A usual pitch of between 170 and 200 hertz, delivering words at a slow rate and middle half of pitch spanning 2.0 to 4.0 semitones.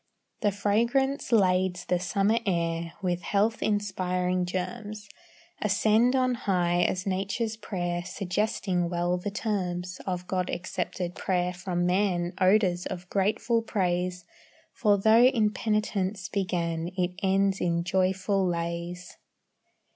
Yes: medium, 185 Hz; slow, 120 wpm; average, 2.7 semitones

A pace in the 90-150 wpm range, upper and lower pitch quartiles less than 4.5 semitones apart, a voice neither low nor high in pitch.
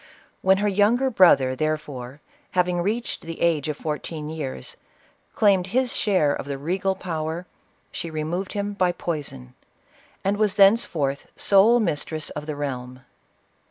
No: average, 145 wpm; average, 4.8 semitones; medium, 170 Hz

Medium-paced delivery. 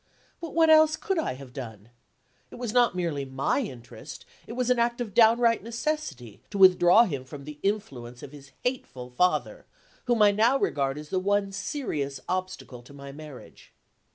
Yes: average, 180 wpm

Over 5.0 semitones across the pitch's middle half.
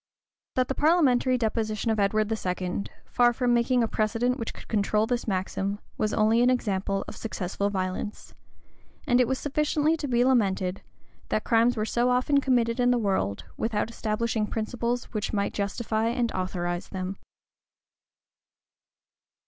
No: average, 3.5 semitones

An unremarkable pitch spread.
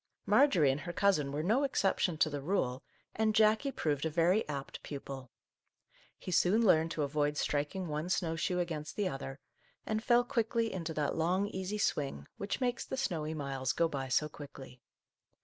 No: wide, 5.8 semitones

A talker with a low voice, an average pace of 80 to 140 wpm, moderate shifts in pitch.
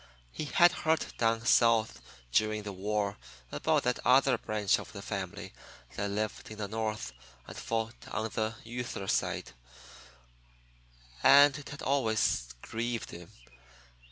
No: low, 110 Hz; slow, 135 wpm; narrow, 2.1 semitones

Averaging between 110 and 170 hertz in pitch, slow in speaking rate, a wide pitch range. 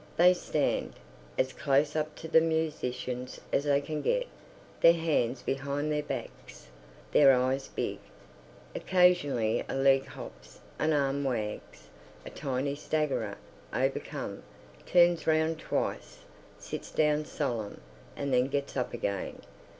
No: medium, 140 Hz; slow, 125 wpm; average, 3.2 semitones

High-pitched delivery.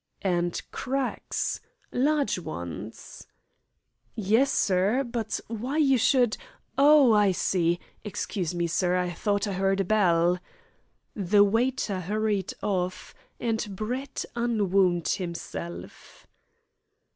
Yes: high, 205 Hz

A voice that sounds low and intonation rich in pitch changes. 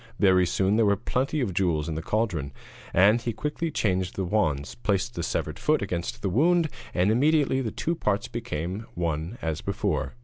Yes: low, 100 Hz; wide, 5.7 semitones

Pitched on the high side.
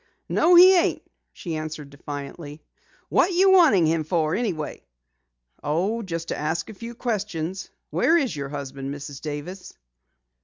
No: medium, 165 Hz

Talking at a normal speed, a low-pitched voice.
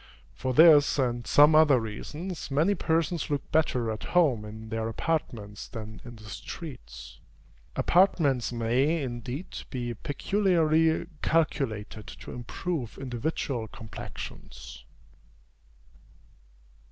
No: slow, 105 wpm; low, 130 Hz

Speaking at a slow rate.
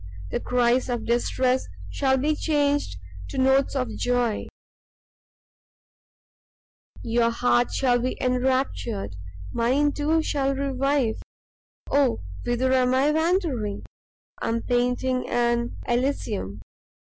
Yes: slow, 105 wpm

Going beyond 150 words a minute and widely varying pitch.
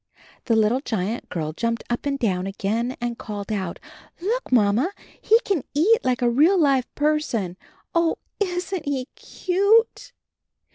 No: average, 145 wpm; wide, 7.7 semitones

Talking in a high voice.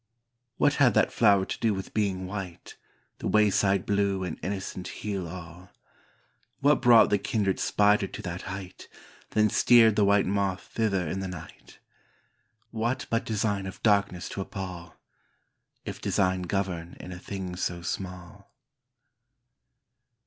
No: very low, 95 Hz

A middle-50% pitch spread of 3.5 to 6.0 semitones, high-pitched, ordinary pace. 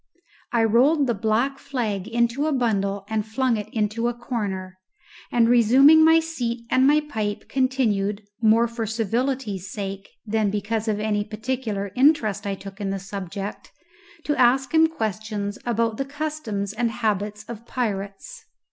Yes: average, 3.9 semitones; high, 225 Hz; average, 155 wpm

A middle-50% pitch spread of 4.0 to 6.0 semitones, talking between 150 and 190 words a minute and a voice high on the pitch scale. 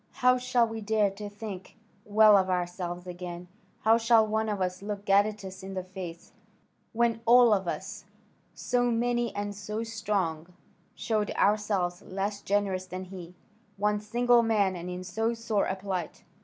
No: average, 3.1 semitones; average, 160 wpm; high, 205 Hz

